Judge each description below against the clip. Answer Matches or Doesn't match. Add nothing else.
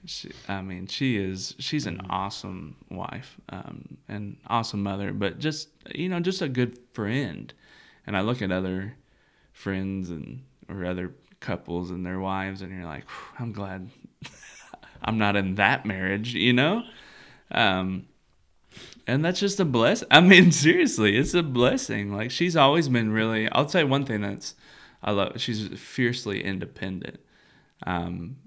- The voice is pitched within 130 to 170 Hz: Doesn't match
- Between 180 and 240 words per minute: Doesn't match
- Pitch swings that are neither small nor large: Doesn't match